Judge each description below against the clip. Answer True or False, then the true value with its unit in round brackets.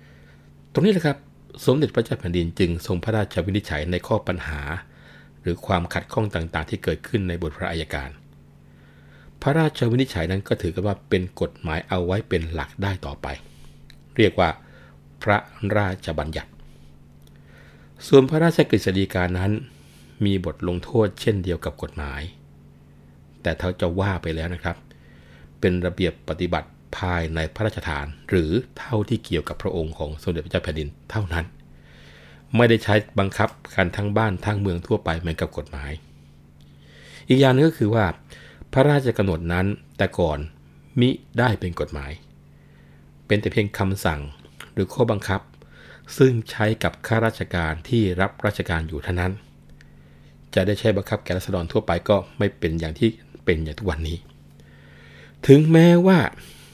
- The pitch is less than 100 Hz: True (85 Hz)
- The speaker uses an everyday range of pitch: False (5.8 semitones)